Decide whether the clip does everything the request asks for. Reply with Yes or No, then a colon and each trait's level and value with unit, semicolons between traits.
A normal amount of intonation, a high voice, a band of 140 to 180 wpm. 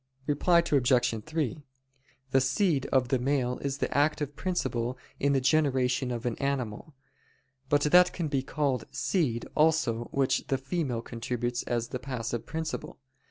No: average, 3.5 semitones; low, 135 Hz; average, 150 wpm